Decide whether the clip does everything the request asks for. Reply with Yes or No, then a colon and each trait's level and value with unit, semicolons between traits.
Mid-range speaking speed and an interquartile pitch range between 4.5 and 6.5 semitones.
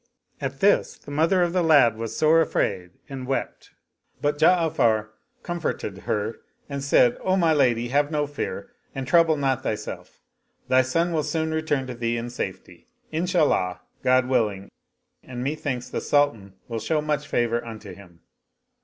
Yes: average, 170 wpm; average, 5.1 semitones